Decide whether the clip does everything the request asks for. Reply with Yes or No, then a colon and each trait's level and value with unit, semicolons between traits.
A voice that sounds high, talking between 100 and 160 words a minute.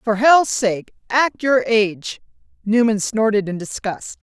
Yes: high, 220 Hz; average, 140 wpm